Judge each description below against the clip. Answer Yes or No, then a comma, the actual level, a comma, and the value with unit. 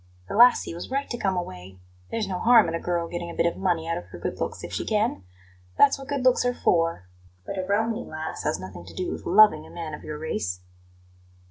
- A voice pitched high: No, medium, 175 Hz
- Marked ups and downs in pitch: Yes, wide, 5.9 semitones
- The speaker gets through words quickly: Yes, fast, 245 wpm